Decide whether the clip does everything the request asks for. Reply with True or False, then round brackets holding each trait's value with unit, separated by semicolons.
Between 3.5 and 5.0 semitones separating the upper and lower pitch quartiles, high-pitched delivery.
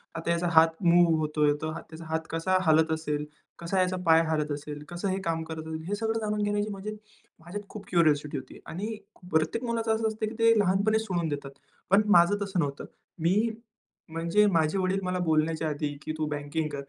False (4.2 semitones; 170 Hz)